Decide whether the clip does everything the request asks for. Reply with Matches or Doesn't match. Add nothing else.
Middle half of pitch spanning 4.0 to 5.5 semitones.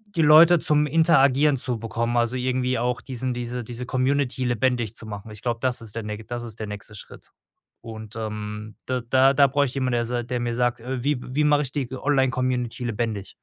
Doesn't match